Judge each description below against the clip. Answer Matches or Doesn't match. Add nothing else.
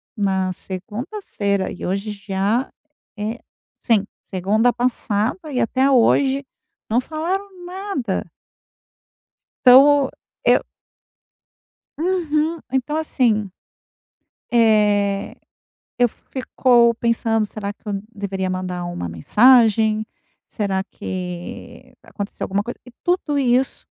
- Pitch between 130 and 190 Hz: Doesn't match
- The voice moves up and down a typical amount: Matches